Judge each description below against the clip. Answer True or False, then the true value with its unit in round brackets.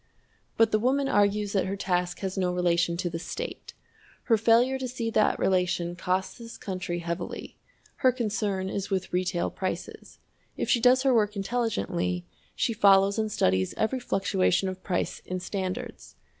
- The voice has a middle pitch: False (195 Hz)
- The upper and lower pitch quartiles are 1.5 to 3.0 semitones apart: False (3.9 semitones)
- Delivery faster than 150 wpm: True (165 wpm)